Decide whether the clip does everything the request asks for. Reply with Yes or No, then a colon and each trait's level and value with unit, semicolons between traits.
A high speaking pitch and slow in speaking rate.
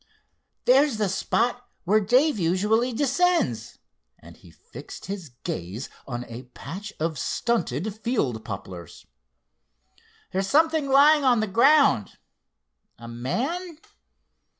Yes: high, 210 Hz; slow, 110 wpm